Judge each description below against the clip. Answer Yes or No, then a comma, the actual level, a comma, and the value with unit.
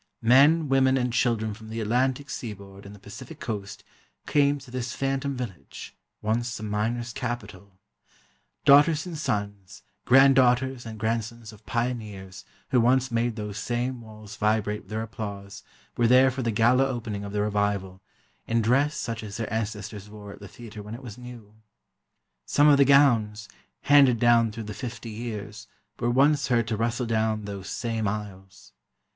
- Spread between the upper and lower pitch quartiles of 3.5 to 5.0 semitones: No, average, 3.1 semitones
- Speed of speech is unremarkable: Yes, average, 165 wpm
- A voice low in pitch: Yes, low, 115 Hz